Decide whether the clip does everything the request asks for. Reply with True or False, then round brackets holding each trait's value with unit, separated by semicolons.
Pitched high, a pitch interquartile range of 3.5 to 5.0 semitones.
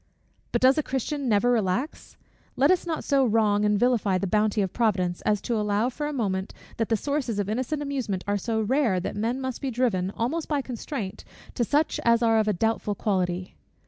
True (225 Hz; 4.3 semitones)